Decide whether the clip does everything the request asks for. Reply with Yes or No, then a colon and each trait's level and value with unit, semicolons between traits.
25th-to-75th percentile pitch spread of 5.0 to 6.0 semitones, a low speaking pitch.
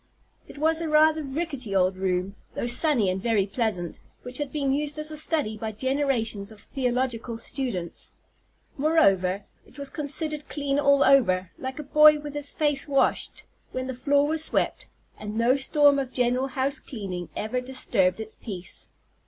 No: average, 5.3 semitones; very high, 260 Hz